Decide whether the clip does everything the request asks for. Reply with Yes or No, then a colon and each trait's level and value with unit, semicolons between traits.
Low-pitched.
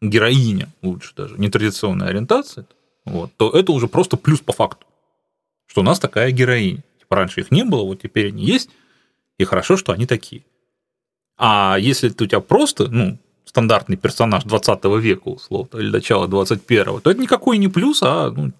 Yes: low, 120 Hz